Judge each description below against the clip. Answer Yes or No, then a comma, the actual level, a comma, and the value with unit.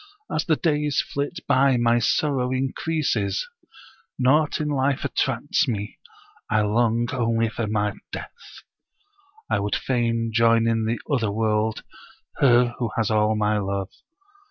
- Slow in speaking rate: Yes, slow, 130 wpm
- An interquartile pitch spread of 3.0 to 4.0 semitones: Yes, average, 3.6 semitones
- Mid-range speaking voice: No, low, 120 Hz